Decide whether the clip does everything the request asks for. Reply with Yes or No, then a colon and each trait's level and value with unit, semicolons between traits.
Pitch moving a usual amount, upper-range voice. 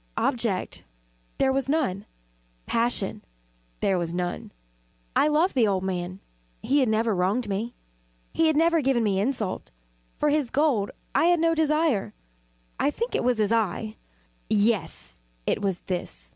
No: wide, 6.9 semitones; high, 230 Hz